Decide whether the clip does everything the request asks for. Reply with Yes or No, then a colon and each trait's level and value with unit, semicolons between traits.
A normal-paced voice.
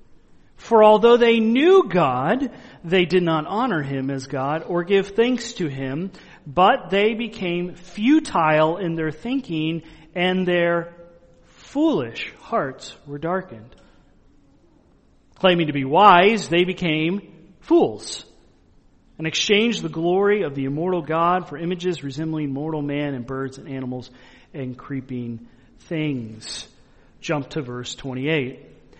No: slow, 125 wpm